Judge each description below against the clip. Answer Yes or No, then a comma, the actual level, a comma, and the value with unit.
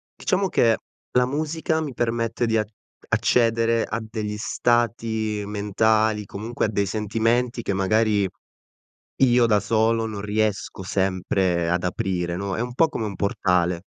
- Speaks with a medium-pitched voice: No, low, 110 Hz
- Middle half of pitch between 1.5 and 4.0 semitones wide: Yes, average, 2.7 semitones